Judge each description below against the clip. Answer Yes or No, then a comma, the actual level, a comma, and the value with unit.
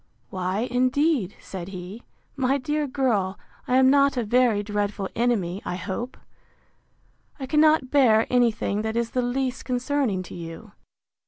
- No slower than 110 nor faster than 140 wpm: No, average, 150 wpm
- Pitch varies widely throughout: No, average, 4.6 semitones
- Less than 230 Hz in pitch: No, high, 240 Hz